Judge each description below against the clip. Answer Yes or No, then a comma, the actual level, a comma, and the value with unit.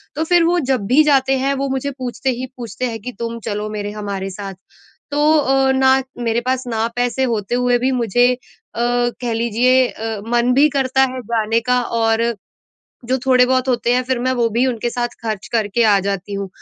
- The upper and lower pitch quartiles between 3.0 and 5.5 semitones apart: No, narrow, 2.6 semitones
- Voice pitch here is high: Yes, high, 245 Hz